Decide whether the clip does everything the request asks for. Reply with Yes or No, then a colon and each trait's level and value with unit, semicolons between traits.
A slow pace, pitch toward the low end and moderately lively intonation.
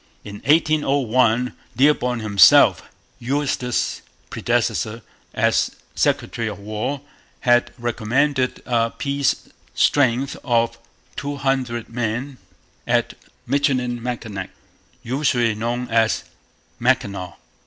Yes: slow, 85 wpm; low, 125 Hz; average, 3.0 semitones